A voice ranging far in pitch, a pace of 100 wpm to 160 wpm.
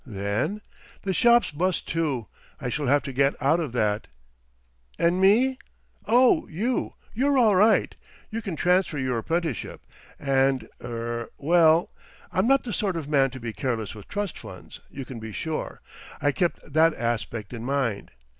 Yes: wide, 7.5 semitones; average, 155 wpm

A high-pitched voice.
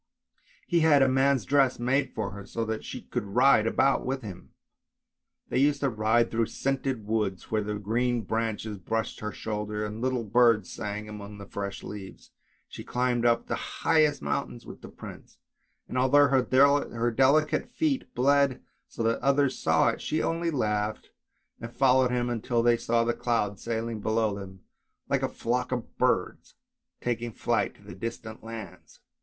No: low, 115 Hz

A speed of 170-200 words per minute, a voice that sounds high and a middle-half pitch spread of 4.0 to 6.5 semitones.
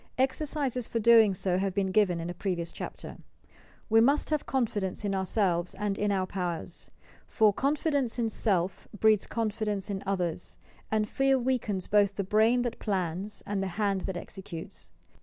No: average, 175 wpm; high, 205 Hz; average, 3.3 semitones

